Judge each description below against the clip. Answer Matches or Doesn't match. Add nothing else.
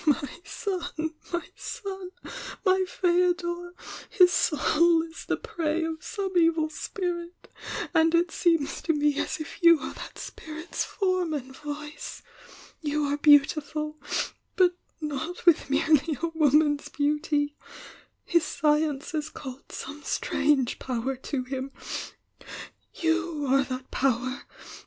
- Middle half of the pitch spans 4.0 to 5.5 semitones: Doesn't match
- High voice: Matches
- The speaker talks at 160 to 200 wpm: Doesn't match